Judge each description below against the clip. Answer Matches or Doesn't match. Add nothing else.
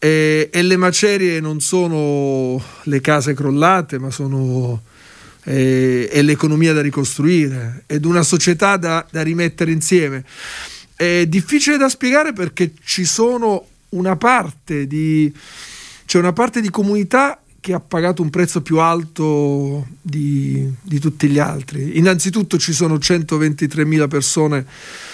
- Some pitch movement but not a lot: Matches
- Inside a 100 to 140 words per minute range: Matches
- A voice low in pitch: Doesn't match